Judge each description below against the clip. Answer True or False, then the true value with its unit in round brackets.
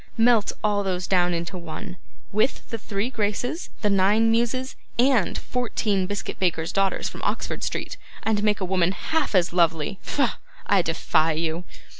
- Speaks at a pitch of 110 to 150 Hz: False (200 Hz)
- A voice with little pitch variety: False (4.0 semitones)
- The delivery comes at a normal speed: True (160 wpm)